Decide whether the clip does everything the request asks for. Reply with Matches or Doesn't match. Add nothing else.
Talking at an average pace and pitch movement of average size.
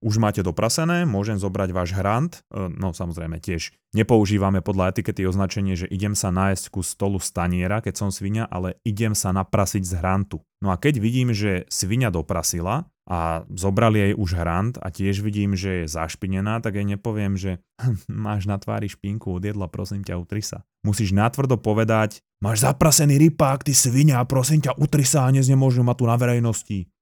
Doesn't match